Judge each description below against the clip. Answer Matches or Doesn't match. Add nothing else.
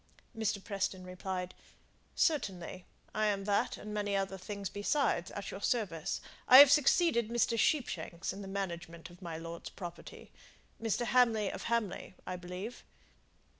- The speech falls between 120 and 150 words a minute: Matches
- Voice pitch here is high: Matches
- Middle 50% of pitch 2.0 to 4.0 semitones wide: Matches